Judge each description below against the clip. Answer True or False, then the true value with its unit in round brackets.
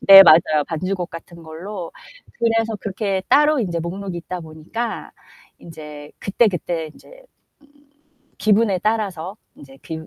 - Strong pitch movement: False (4.9 semitones)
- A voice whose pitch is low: False (185 Hz)